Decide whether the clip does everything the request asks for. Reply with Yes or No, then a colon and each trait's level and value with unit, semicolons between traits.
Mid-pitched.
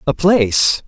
Yes: medium, 160 Hz